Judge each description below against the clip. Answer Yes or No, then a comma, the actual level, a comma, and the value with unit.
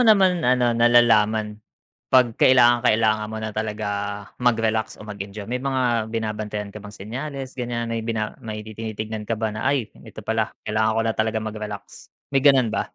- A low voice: Yes, low, 110 Hz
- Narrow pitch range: Yes, narrow, 2.1 semitones